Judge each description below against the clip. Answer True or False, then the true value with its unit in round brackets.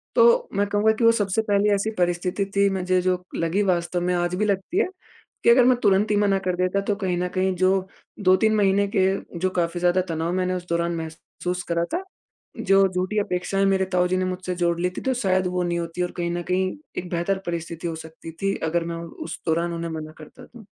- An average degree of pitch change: False (2.2 semitones)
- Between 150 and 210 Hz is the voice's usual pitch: True (185 Hz)